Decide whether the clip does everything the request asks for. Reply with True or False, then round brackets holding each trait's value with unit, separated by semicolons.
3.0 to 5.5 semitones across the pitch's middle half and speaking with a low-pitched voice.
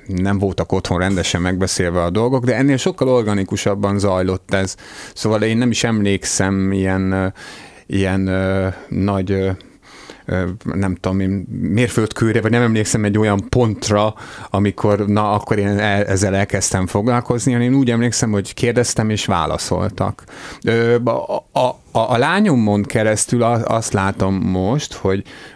True (3.3 semitones; 105 Hz)